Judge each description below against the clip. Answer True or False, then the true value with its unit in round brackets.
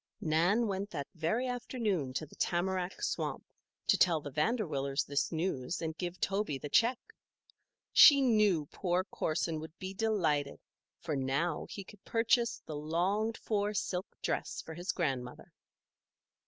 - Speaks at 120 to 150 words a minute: True (145 wpm)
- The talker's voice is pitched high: False (175 Hz)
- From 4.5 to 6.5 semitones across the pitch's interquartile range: True (5.3 semitones)